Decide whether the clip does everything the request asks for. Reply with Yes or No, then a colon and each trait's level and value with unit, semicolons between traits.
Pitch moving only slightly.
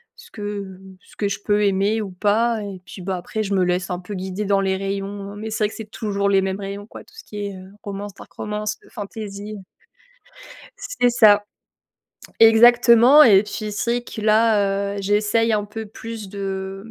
Yes: narrow, 1.8 semitones